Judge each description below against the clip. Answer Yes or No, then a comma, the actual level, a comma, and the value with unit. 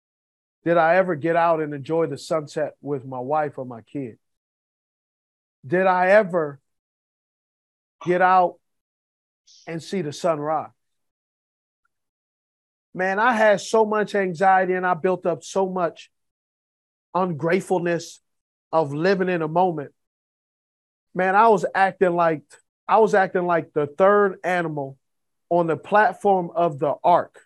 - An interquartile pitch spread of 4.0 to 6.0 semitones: Yes, average, 4.4 semitones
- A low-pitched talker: No, medium, 170 Hz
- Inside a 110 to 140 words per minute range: Yes, slow, 135 wpm